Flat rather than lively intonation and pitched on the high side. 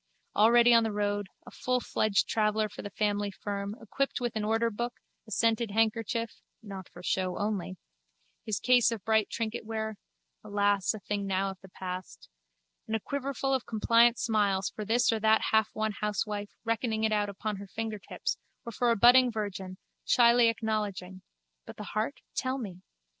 Yes: narrow, 2.1 semitones; high, 215 Hz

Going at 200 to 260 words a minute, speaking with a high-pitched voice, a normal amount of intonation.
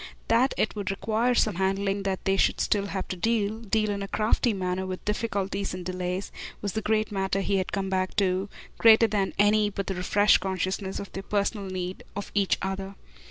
No: fast, 205 wpm; high, 195 Hz; narrow, 1.8 semitones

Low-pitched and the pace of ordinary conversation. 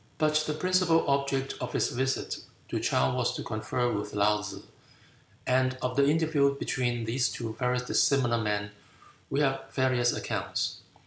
Yes: low, 130 Hz; average, 155 wpm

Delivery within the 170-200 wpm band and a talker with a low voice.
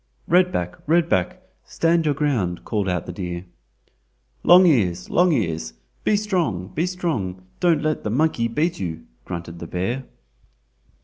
No: average, 145 wpm; low, 120 Hz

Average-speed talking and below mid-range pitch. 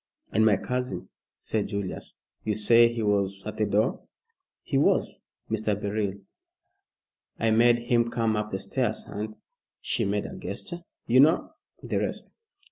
Yes: average, 150 wpm; low, 110 Hz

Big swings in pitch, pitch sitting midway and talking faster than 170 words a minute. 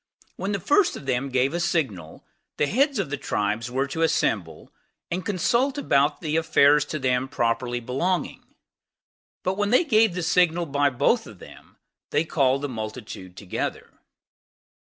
No: wide, 6.4 semitones; medium, 145 Hz; average, 160 wpm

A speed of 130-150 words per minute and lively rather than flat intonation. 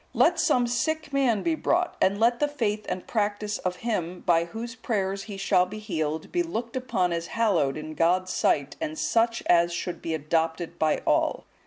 No: average, 190 wpm; wide, 5.7 semitones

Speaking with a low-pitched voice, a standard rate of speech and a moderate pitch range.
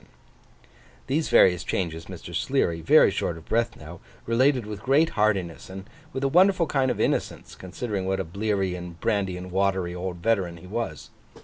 Yes: very low, 95 Hz; average, 175 wpm; average, 4.8 semitones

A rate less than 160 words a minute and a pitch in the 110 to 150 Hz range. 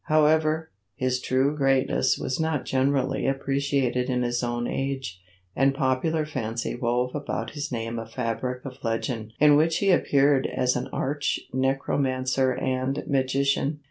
Yes: average, 140 wpm; low, 135 Hz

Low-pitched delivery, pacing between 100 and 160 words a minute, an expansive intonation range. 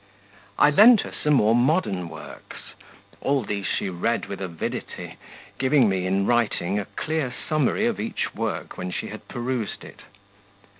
Yes: low, 120 Hz; average, 155 wpm; wide, 7.2 semitones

